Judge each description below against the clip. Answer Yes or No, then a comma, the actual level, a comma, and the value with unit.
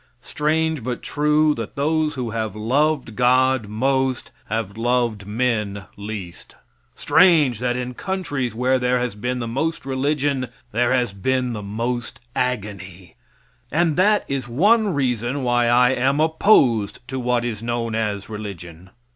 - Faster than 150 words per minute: No, average, 145 wpm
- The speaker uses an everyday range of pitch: Yes, average, 3.9 semitones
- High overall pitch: No, low, 125 Hz